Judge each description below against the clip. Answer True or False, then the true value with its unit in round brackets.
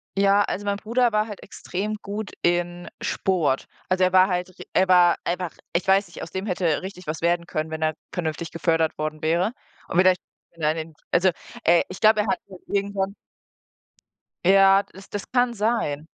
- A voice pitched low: False (185 Hz)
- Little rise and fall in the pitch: False (3.1 semitones)